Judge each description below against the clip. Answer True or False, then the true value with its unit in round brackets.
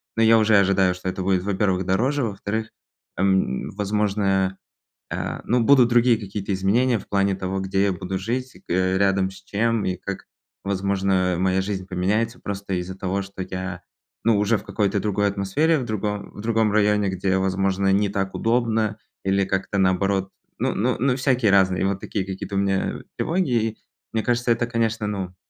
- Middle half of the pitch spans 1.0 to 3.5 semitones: True (2.6 semitones)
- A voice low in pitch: True (100 Hz)